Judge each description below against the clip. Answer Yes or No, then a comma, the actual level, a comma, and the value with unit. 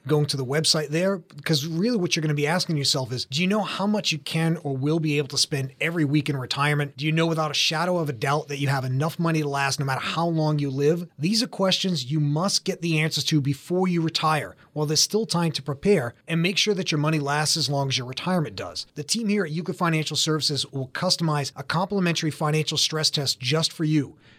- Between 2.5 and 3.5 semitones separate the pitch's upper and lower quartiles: Yes, average, 2.8 semitones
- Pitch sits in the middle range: Yes, medium, 155 Hz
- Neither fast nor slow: No, fast, 250 wpm